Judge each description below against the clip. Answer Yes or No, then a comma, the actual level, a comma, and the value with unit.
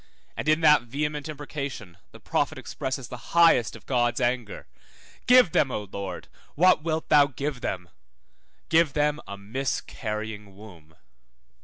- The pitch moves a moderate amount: No, wide, 5.9 semitones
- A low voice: Yes, low, 130 Hz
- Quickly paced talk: No, average, 140 wpm